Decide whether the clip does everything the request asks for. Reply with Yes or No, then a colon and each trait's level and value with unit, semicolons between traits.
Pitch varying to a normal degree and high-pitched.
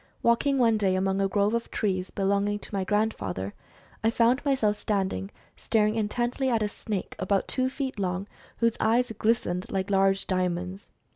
Yes: average, 3.2 semitones; high, 205 Hz